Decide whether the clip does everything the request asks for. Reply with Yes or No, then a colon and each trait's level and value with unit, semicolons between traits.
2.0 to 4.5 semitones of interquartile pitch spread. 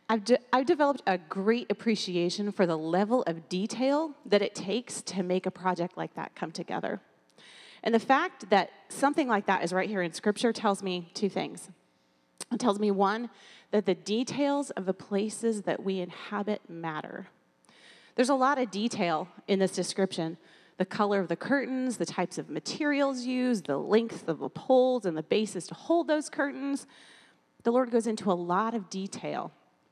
No: average, 5.2 semitones